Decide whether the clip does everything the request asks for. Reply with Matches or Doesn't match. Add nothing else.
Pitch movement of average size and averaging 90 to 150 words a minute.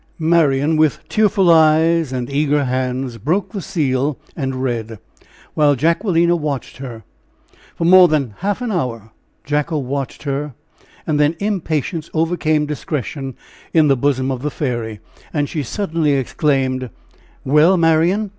Matches